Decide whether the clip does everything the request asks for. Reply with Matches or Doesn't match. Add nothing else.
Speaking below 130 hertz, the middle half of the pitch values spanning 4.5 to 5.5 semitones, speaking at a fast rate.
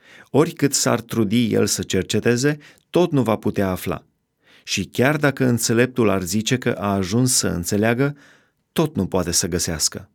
Doesn't match